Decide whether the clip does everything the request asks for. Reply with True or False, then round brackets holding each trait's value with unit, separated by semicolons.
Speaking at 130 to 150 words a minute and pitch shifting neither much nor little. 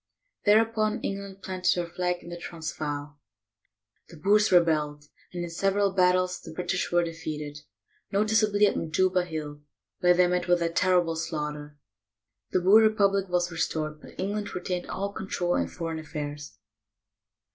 True (145 wpm; 3.6 semitones)